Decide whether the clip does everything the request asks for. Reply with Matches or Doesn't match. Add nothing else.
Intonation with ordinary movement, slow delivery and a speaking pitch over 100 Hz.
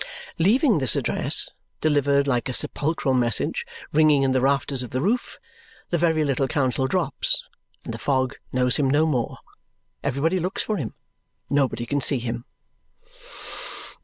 Doesn't match